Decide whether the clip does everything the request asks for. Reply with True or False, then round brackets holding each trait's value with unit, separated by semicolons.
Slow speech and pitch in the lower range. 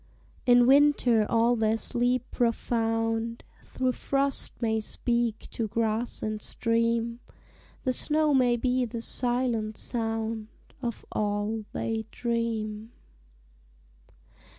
False (105 wpm; 230 Hz)